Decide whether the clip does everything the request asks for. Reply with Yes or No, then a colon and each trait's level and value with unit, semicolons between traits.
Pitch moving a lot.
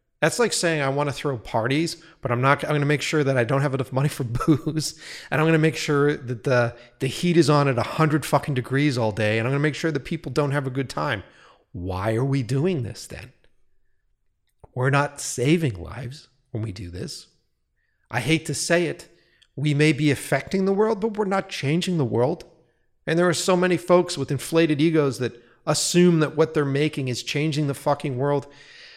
No: average, 3.5 semitones